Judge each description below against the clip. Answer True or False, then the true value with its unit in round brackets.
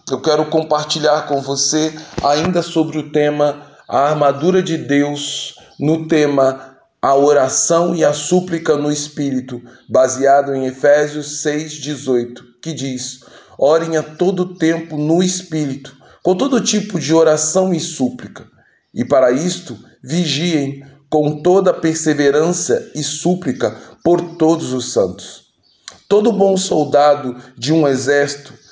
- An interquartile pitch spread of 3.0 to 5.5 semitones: False (2.6 semitones)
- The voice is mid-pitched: True (150 Hz)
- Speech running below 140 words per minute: True (125 wpm)